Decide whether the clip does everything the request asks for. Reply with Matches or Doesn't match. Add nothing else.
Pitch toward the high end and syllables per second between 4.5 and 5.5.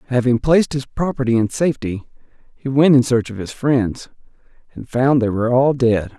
Doesn't match